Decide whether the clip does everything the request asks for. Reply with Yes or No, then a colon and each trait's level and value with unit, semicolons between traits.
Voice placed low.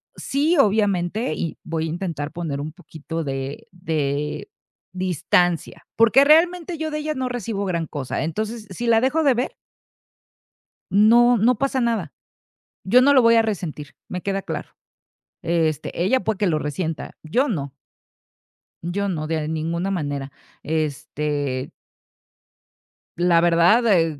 No: medium, 180 Hz